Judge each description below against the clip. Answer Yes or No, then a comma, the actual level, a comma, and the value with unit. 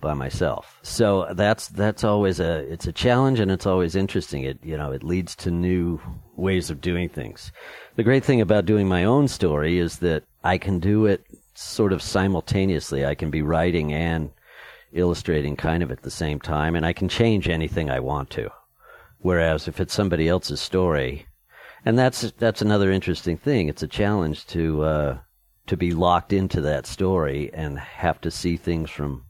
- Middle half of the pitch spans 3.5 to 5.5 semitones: Yes, average, 3.8 semitones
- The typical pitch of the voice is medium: No, very low, 85 Hz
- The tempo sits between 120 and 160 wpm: No, average, 185 wpm